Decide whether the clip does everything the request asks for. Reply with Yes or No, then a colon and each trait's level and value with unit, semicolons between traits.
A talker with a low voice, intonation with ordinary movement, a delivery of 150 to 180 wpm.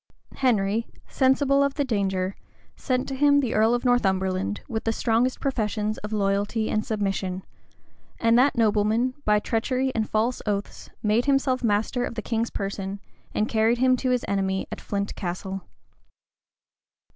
No: high, 220 Hz; average, 3.9 semitones; average, 155 wpm